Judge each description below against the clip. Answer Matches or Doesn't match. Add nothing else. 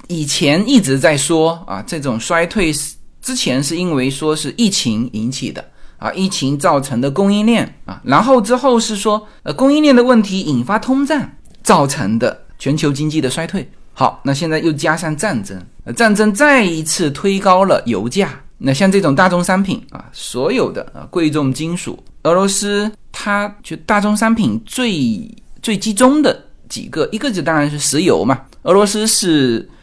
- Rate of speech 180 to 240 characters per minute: Doesn't match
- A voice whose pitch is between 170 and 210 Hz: Matches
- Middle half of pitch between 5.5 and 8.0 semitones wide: Matches